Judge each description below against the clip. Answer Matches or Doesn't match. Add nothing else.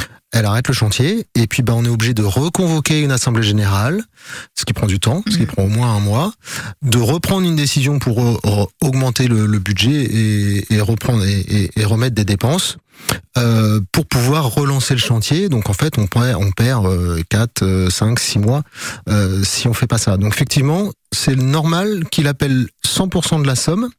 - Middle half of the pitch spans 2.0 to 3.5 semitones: Doesn't match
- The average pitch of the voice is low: Matches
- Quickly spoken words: Doesn't match